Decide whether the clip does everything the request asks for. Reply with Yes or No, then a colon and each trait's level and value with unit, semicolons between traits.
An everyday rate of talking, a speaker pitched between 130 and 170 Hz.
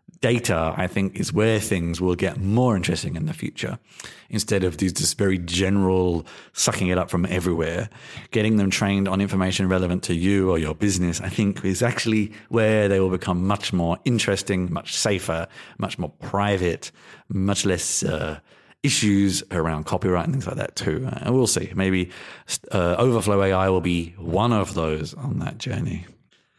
No: average, 170 wpm; very low, 95 Hz